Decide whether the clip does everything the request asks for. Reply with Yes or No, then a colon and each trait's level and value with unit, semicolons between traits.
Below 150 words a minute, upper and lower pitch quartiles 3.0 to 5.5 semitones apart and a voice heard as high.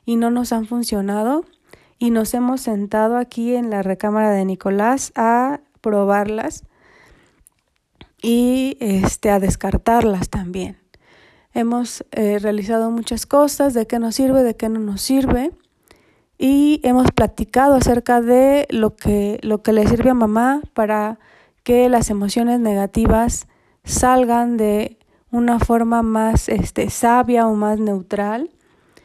No: average, 130 wpm; narrow, 2.5 semitones; high, 230 Hz